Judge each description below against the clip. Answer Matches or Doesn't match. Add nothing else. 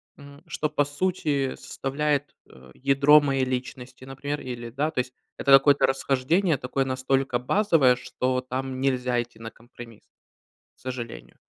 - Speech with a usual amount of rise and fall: Doesn't match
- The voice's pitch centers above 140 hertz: Doesn't match